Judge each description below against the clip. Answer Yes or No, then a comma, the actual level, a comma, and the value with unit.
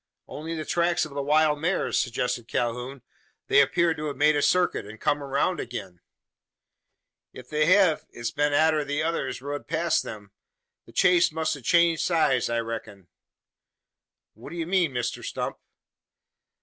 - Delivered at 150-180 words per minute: Yes, average, 160 wpm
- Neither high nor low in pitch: Yes, medium, 150 Hz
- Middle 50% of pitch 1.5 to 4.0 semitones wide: No, average, 4.9 semitones